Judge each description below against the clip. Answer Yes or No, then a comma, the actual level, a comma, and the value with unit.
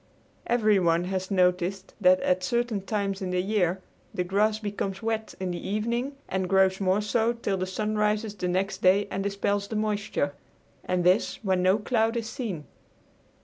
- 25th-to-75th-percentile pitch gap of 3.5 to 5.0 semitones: No, narrow, 2.5 semitones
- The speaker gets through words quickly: No, average, 175 wpm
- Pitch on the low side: No, high, 195 Hz